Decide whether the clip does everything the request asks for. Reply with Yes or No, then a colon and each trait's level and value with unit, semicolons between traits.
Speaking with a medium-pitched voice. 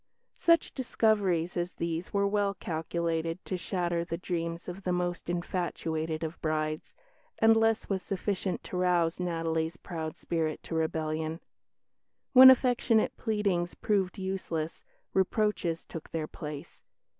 Yes: medium, 175 Hz